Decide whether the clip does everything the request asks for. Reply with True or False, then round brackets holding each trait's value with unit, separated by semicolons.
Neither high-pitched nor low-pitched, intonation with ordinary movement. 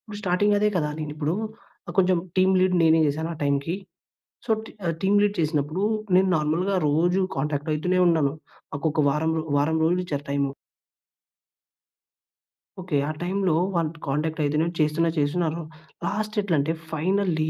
True (160 Hz; 3.4 semitones)